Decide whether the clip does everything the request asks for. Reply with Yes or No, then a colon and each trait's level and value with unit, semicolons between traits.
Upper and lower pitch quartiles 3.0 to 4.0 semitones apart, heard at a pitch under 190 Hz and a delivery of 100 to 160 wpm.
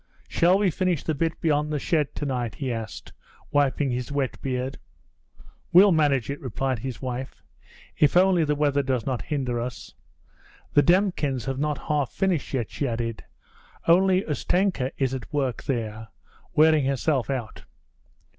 Yes: average, 3.6 semitones; medium, 140 Hz; average, 155 wpm